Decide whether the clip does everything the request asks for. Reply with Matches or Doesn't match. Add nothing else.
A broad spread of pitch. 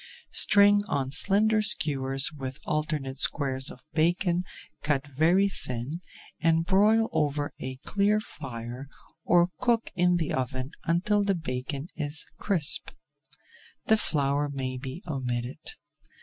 Matches